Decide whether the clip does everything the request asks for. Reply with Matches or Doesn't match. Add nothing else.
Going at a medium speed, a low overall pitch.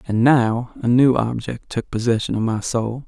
Matches